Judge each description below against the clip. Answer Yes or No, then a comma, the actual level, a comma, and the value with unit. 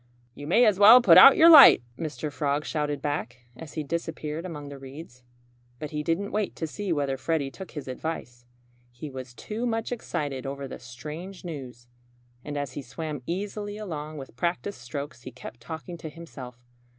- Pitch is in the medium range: Yes, medium, 150 Hz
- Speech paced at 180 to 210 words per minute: Yes, average, 185 wpm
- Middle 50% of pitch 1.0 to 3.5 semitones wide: No, average, 4.3 semitones